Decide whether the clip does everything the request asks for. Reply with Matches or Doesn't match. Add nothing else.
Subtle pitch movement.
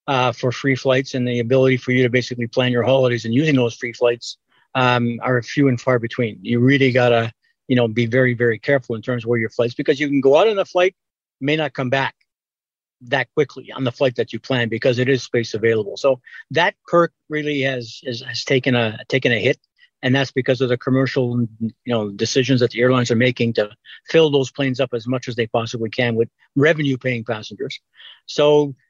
Matches